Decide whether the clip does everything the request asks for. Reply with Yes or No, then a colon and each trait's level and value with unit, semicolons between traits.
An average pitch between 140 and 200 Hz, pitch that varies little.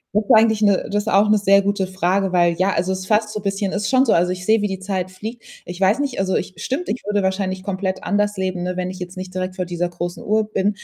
Yes: high, 190 Hz; narrow, 2.1 semitones